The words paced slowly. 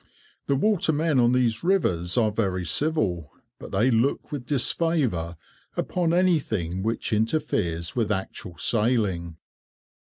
Yes: slow, 120 wpm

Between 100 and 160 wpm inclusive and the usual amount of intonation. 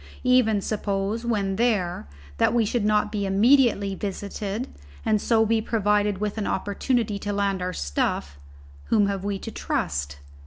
No: average, 155 wpm; narrow, 2.2 semitones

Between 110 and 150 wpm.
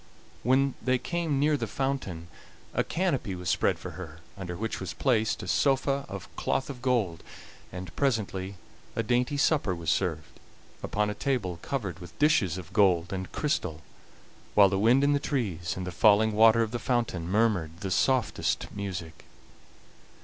No: average, 165 wpm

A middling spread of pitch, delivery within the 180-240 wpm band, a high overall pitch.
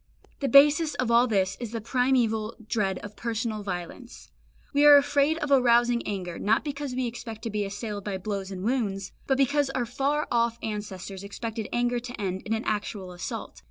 Yes: average, 4.0 semitones; average, 190 wpm; high, 230 Hz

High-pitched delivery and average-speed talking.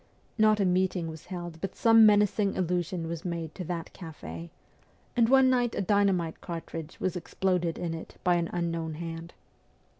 No: medium, 175 Hz; average, 170 wpm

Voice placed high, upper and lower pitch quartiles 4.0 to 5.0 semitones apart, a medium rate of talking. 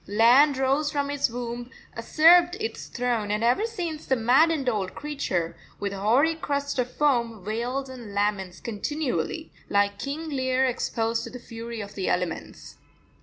Yes: very high, 250 Hz; average, 4.7 semitones; average, 155 wpm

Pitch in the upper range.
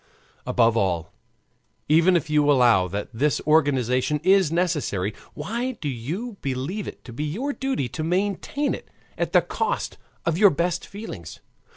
No: medium, 150 Hz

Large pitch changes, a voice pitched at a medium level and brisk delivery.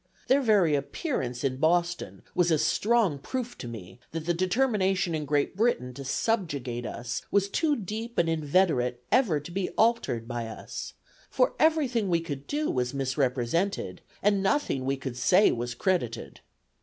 No: wide, 8.3 semitones; medium, 165 Hz; average, 165 wpm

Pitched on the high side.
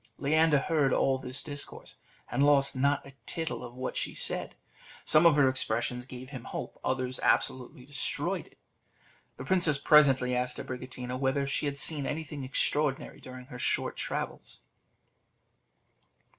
No: low, 135 Hz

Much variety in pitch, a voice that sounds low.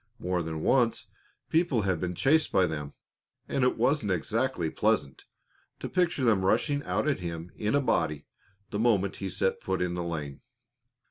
Yes: wide, 6.6 semitones; very low, 95 Hz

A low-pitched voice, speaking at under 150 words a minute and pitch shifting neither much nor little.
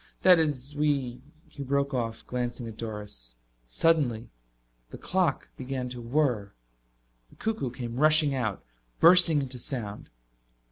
Yes: low, 130 Hz; slow, 135 wpm; average, 4.1 semitones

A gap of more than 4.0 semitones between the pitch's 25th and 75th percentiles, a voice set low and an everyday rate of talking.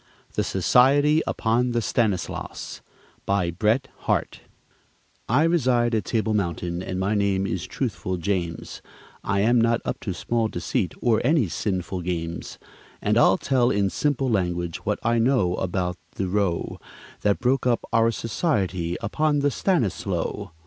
Yes: average, 4.8 semitones; low, 105 Hz; average, 145 wpm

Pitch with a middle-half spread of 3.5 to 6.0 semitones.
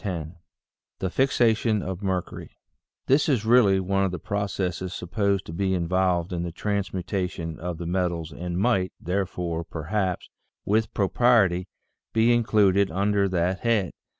No: narrow, 2.6 semitones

